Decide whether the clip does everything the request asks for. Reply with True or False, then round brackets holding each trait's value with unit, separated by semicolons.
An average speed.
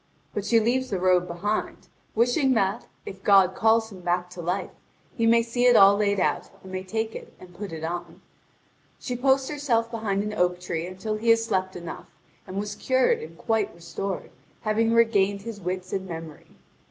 True (190 wpm)